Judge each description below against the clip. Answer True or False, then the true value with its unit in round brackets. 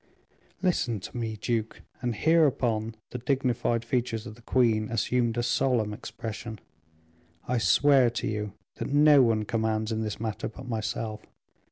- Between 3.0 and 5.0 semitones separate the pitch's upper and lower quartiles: False (2.4 semitones)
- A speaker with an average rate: True (155 wpm)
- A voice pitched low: True (115 Hz)